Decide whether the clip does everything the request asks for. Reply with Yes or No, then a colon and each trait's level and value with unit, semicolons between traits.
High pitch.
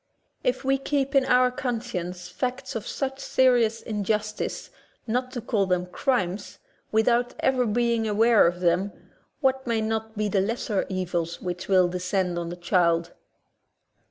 Yes: high, 220 Hz